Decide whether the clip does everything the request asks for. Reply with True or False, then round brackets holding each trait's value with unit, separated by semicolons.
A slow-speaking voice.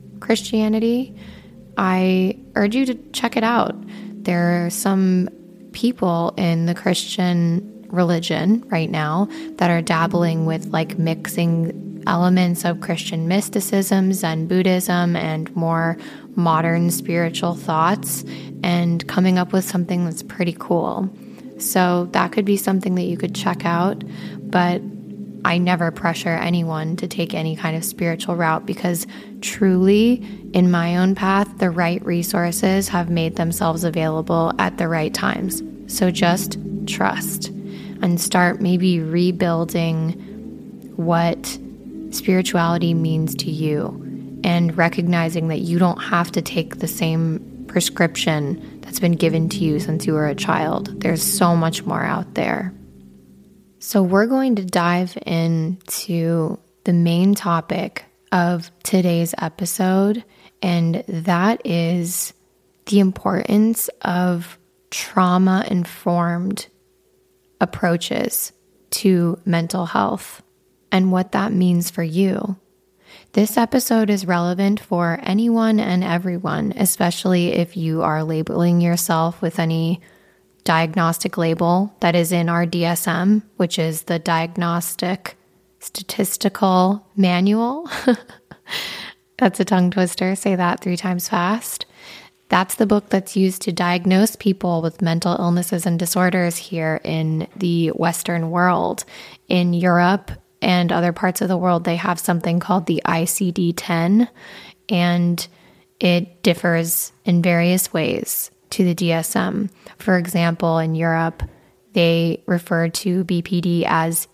True (125 wpm)